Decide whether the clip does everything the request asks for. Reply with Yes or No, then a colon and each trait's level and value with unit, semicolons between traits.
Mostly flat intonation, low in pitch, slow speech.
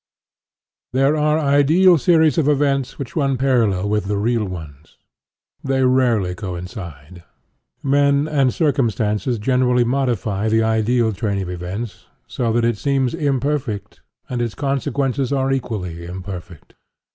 No: average, 5.2 semitones; low, 120 Hz; slow, 130 wpm